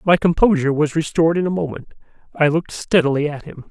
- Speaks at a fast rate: No, average, 195 wpm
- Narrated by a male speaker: Yes, male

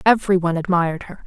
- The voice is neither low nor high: Yes, medium, 180 Hz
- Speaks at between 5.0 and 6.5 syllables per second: No, 7.7 syllables/s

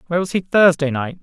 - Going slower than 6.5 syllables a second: No, 6.9 syllables/s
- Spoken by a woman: No, male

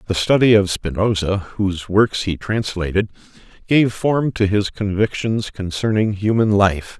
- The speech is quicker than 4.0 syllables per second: No, 3.8 syllables/s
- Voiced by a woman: No, male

